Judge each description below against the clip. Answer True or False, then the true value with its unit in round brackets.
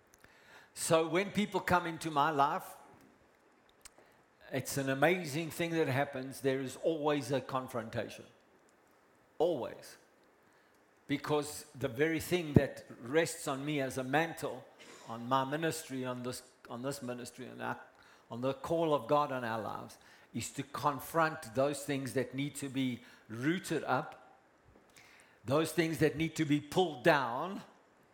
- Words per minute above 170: False (145 wpm)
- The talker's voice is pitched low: False (145 Hz)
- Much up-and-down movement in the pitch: False (3.5 semitones)